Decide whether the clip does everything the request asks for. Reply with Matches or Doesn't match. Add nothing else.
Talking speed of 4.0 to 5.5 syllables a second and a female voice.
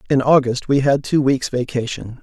Doesn't match